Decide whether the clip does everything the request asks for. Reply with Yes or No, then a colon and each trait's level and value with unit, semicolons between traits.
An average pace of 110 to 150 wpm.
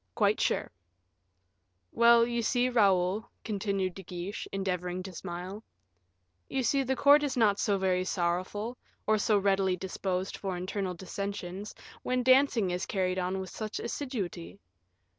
Yes: average, 140 wpm